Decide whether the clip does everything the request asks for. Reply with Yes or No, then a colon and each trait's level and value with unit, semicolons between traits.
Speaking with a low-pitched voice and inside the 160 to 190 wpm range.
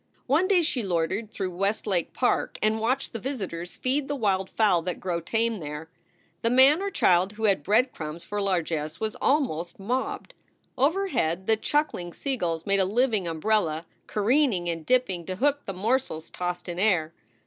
No: high, 200 Hz; average, 170 wpm